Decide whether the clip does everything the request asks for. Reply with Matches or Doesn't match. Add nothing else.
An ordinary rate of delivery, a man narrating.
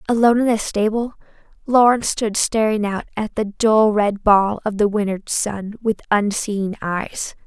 Doesn't match